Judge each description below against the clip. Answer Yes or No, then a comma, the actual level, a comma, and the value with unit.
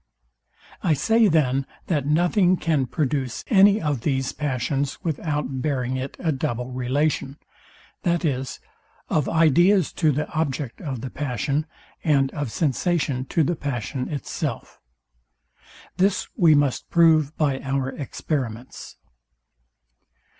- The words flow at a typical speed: No, slow, 120 wpm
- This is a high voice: No, medium, 145 Hz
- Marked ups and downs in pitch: No, average, 3.5 semitones